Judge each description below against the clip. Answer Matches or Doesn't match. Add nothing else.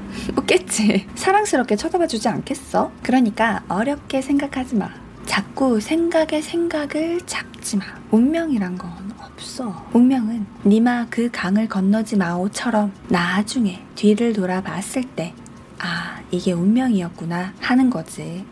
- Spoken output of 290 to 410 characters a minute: Doesn't match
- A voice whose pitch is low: Doesn't match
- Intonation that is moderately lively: Matches